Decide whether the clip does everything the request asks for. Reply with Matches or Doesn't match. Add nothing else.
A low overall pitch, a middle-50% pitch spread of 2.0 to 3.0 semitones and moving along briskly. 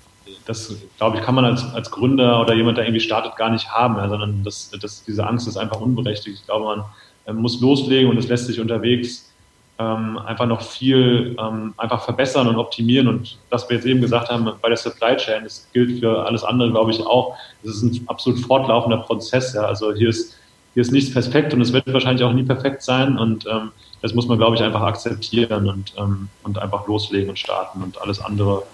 Matches